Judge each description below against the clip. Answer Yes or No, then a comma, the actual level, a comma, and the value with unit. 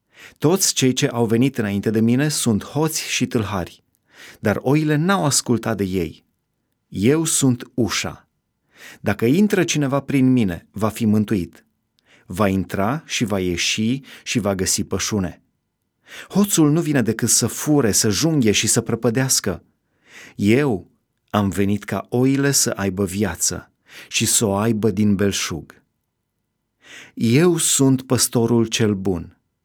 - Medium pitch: No, low, 115 Hz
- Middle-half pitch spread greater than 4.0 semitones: Yes, average, 4.9 semitones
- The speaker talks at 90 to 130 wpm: No, average, 140 wpm